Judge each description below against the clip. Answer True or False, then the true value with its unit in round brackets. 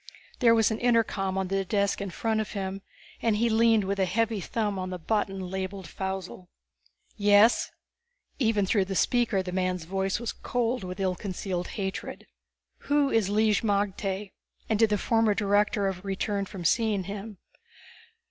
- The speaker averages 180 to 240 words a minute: False (165 wpm)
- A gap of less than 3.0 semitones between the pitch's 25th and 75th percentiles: True (2.6 semitones)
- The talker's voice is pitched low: False (200 Hz)